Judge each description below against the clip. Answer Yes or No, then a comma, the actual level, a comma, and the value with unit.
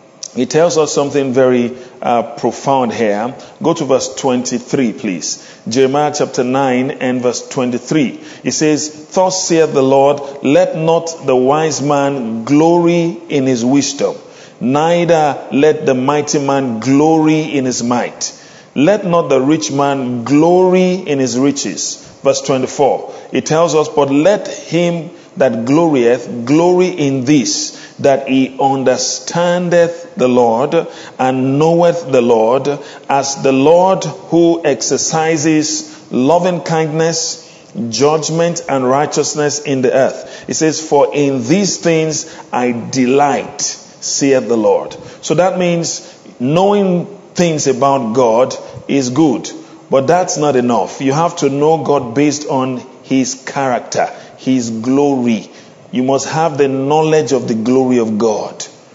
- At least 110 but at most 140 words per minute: Yes, slow, 135 wpm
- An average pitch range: Yes, average, 3.9 semitones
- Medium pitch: Yes, medium, 145 Hz